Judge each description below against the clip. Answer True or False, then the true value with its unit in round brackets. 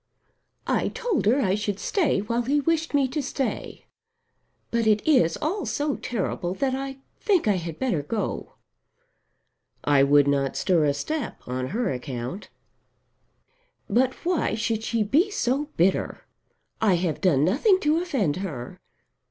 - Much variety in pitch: True (9.0 semitones)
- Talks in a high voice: True (220 Hz)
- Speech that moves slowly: False (150 wpm)